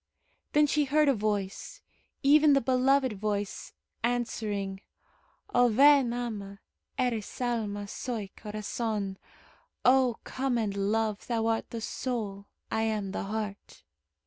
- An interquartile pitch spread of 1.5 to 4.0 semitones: Yes, average, 3.7 semitones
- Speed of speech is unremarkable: No, slow, 120 wpm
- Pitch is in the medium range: No, high, 225 Hz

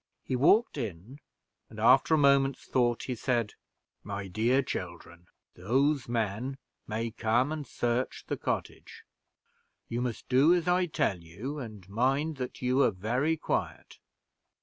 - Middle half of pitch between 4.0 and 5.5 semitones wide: Yes, average, 4.3 semitones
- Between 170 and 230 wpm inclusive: No, average, 145 wpm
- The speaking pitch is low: Yes, low, 125 Hz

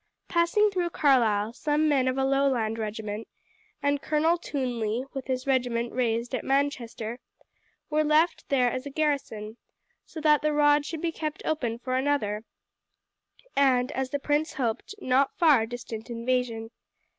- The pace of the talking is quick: No, average, 150 wpm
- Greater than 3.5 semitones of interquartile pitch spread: Yes, average, 4.1 semitones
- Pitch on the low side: No, very high, 265 Hz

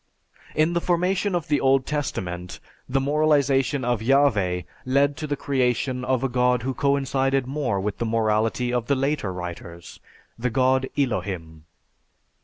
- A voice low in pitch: Yes, low, 130 Hz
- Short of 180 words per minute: Yes, average, 155 wpm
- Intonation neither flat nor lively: Yes, average, 4.2 semitones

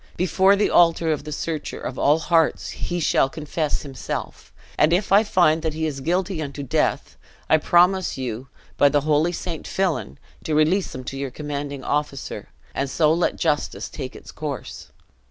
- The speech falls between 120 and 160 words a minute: No, average, 175 wpm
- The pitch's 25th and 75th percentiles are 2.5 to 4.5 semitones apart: Yes, average, 3.4 semitones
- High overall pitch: No, medium, 155 Hz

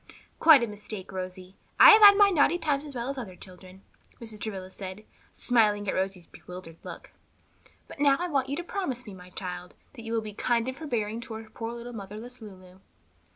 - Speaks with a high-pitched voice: Yes, high, 220 Hz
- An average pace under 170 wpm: No, average, 200 wpm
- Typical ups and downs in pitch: No, wide, 5.8 semitones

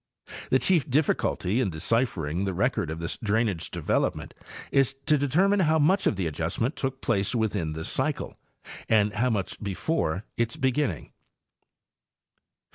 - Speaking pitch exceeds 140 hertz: No, low, 115 Hz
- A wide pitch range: Yes, wide, 6.9 semitones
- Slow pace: No, average, 145 wpm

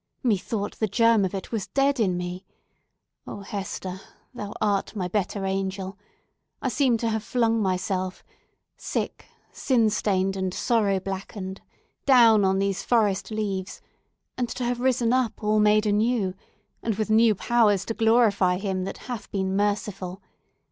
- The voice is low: No, high, 205 Hz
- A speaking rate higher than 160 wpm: No, average, 145 wpm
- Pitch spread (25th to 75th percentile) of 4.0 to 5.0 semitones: No, average, 3.0 semitones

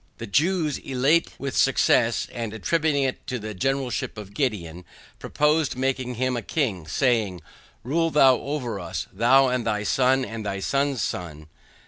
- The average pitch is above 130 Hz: No, low, 125 Hz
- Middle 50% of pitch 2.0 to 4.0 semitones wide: No, average, 4.7 semitones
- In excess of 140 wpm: Yes, average, 155 wpm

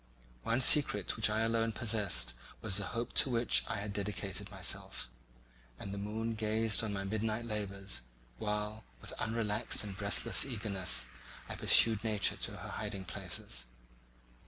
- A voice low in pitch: Yes, low, 105 Hz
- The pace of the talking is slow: No, average, 150 wpm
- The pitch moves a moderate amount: No, narrow, 2.1 semitones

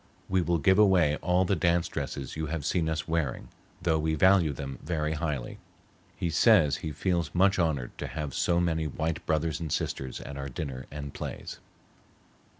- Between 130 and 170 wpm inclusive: No, average, 180 wpm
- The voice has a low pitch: Yes, very low, 80 Hz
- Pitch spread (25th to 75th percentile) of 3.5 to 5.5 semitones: No, average, 2.9 semitones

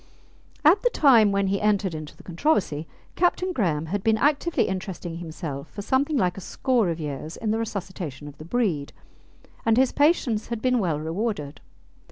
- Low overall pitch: No, high, 200 Hz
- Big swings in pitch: Yes, wide, 7.0 semitones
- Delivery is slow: No, average, 180 wpm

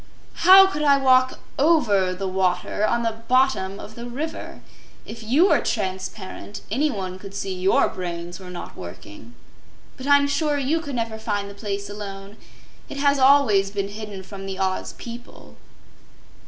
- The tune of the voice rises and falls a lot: Yes, wide, 5.8 semitones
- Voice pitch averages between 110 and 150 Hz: No, high, 210 Hz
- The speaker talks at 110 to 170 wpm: Yes, average, 160 wpm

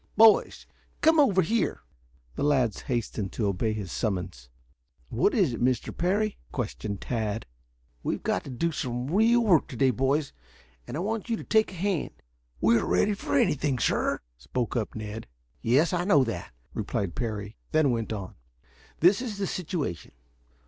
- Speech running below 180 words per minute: Yes, average, 170 wpm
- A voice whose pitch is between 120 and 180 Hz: Yes, low, 135 Hz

